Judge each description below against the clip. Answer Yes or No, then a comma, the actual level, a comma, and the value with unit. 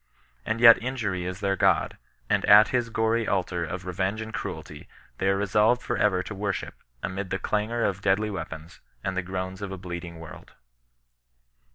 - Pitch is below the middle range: Yes, very low, 95 Hz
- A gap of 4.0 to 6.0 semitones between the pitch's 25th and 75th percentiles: No, average, 2.8 semitones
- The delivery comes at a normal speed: Yes, average, 180 wpm